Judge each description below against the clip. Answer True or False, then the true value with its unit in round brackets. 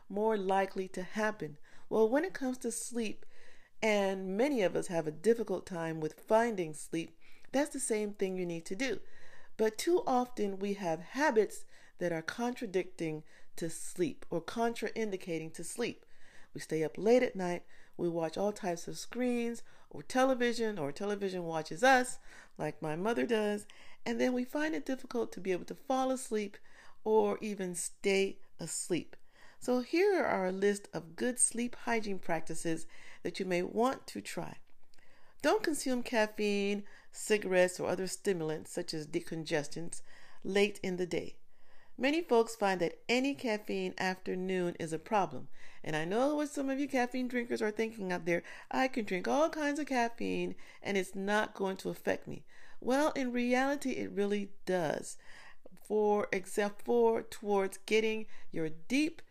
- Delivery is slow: False (165 wpm)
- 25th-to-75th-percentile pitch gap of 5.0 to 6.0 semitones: True (5.3 semitones)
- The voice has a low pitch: False (210 Hz)